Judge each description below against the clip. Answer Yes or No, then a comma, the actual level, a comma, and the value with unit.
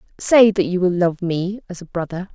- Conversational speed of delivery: No, fast, 230 wpm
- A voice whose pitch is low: No, medium, 185 Hz